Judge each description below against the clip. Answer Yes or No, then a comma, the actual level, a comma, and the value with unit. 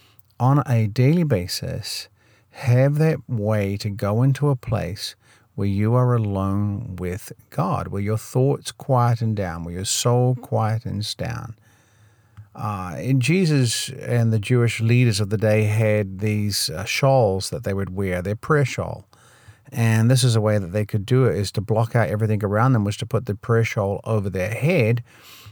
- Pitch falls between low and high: No, low, 110 Hz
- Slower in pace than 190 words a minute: Yes, average, 175 wpm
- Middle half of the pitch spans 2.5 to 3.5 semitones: Yes, average, 3.1 semitones